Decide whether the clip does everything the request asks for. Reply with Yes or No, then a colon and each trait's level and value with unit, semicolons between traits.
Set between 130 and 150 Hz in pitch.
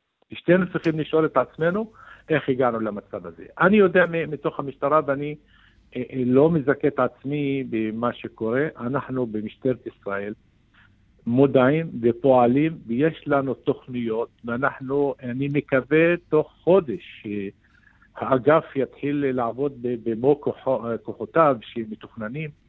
Yes: low, 135 Hz